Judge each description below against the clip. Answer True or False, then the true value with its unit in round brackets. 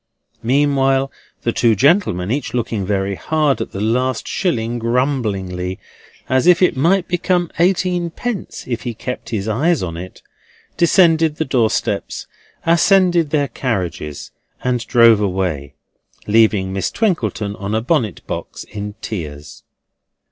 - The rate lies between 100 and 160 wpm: True (135 wpm)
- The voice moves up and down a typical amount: False (7.6 semitones)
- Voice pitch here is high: False (120 Hz)